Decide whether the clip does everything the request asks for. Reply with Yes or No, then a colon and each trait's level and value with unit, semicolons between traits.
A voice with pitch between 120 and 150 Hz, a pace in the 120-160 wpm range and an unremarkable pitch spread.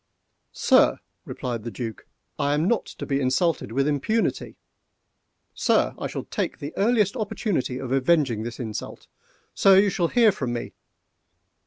No: medium, 140 Hz; average, 140 wpm; wide, 7.8 semitones